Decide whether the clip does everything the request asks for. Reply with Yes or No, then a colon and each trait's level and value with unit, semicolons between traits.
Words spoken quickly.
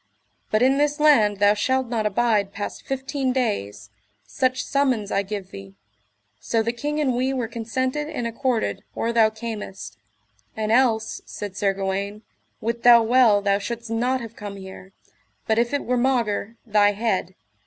No: average, 165 wpm